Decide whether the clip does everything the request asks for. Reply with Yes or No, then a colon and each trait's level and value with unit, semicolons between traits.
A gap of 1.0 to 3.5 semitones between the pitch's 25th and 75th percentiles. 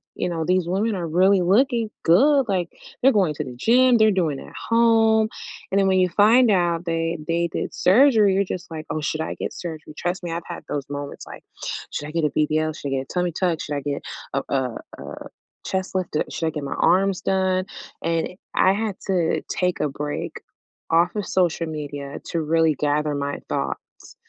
No: average, 4.0 semitones